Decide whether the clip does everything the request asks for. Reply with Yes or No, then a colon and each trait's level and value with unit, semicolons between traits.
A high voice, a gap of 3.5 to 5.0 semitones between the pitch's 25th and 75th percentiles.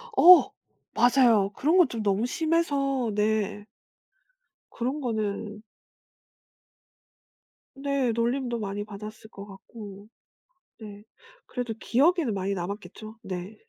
Yes: high, 220 Hz; average, 4.3 semitones